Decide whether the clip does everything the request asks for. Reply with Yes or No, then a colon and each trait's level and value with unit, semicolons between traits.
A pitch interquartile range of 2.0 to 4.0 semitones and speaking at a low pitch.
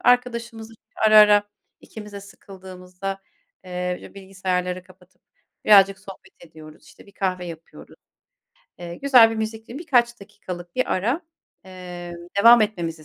No: average, 3.5 semitones; high, 195 Hz